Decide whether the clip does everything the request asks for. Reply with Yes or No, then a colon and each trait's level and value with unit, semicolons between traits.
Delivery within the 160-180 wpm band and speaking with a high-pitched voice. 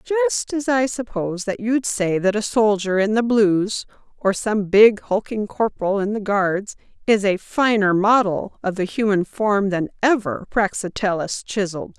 Yes: average, 165 wpm; high, 205 Hz